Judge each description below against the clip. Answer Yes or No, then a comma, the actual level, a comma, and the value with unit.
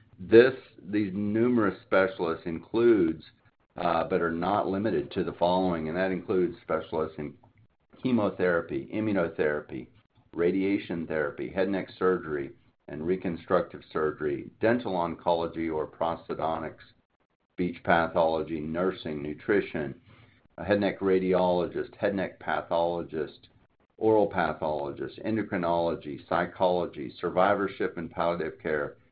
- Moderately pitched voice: No, very low, 90 Hz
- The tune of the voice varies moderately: Yes, average, 3.5 semitones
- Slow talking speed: Yes, slow, 105 wpm